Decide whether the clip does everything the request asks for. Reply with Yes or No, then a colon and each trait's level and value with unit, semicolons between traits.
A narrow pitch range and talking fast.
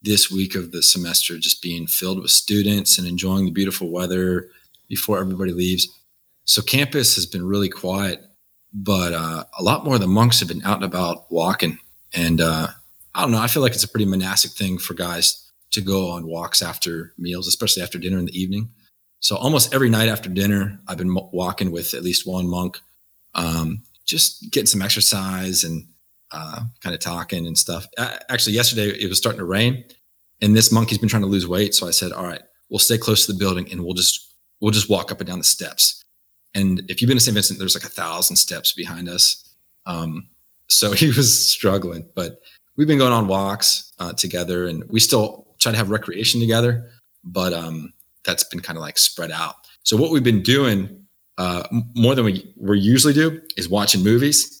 No: average, 3.8 semitones; fast, 210 wpm